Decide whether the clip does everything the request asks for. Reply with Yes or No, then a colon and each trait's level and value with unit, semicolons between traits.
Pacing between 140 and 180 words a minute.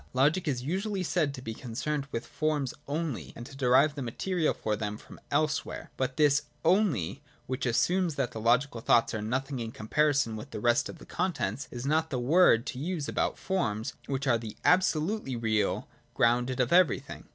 No: average, 190 wpm